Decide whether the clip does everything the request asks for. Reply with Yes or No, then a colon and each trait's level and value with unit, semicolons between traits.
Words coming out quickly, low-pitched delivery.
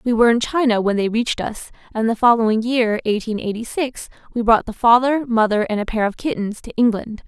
No: fast, 225 wpm; high, 230 Hz